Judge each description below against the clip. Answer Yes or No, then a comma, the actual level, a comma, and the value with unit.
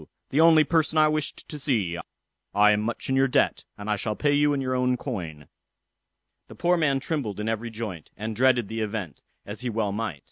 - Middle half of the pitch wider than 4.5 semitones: Yes, wide, 5.4 semitones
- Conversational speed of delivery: No, fast, 220 wpm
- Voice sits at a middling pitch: No, low, 115 Hz